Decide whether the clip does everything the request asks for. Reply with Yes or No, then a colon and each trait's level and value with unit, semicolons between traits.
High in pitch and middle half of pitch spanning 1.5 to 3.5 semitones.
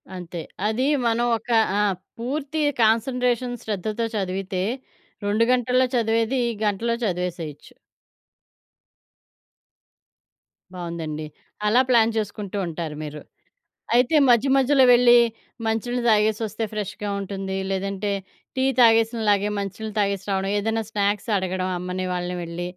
No: high, 210 Hz; average, 3.9 semitones